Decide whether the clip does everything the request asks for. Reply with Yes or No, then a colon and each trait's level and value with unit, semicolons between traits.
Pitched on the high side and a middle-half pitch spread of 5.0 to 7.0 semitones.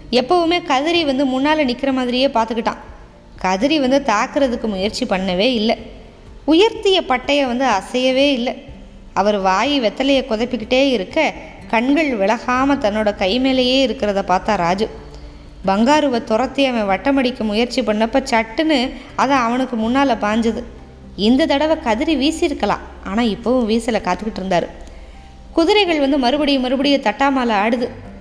No: very high, 250 Hz; average, 4.4 semitones